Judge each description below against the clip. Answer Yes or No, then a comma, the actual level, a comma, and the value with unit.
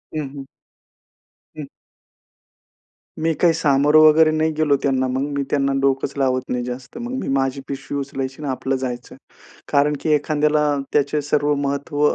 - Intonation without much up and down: Yes, narrow, 2.1 semitones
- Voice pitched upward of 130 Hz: Yes, medium, 140 Hz